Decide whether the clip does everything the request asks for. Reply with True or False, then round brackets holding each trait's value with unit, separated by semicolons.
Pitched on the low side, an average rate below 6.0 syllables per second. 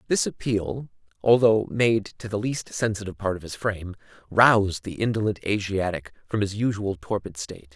True (105 Hz; 5.3 syllables/s)